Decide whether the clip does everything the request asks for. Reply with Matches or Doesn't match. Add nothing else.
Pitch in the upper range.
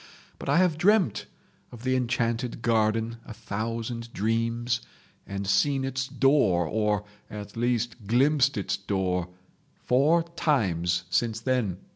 Doesn't match